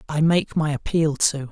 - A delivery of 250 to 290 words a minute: No, average, 200 wpm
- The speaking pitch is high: No, medium, 150 Hz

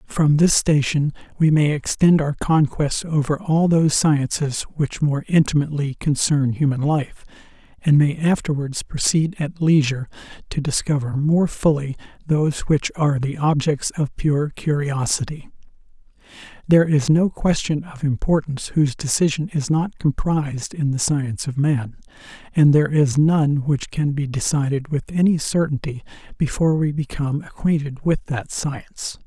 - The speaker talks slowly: No, average, 145 wpm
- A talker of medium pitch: Yes, medium, 145 Hz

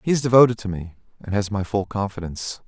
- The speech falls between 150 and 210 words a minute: No, fast, 225 wpm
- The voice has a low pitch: Yes, low, 105 Hz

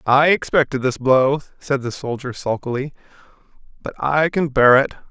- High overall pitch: No, low, 135 Hz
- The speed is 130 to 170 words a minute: Yes, average, 155 wpm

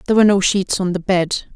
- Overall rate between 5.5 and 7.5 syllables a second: Yes, 6.7 syllables/s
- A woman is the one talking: Yes, female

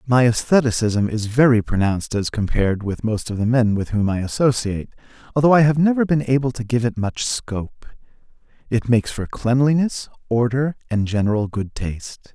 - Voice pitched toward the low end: Yes, low, 115 Hz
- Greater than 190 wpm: No, average, 175 wpm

